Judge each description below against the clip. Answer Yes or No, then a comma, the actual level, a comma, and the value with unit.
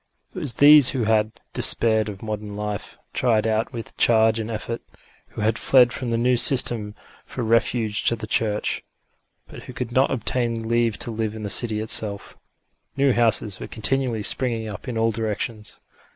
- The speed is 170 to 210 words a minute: Yes, average, 180 wpm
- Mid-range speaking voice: No, low, 115 Hz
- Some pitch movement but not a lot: No, narrow, 2.0 semitones